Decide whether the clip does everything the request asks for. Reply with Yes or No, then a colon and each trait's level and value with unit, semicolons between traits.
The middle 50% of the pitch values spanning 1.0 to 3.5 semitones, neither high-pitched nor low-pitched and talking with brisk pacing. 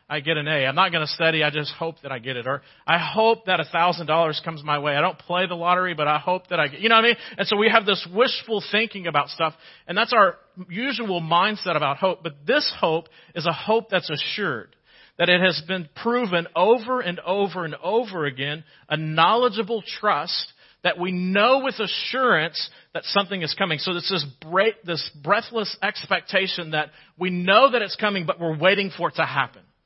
No: average, 4.0 semitones; medium, 180 Hz; fast, 215 wpm